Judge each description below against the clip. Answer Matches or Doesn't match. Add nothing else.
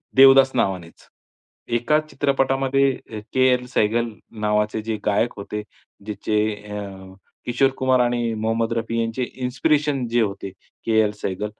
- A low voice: Matches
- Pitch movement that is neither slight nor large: Matches